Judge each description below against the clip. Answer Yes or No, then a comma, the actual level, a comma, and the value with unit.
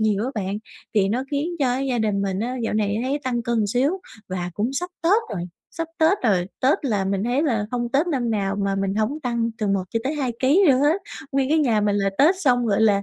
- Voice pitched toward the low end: No, high, 235 Hz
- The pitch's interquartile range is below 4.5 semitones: No, average, 5.0 semitones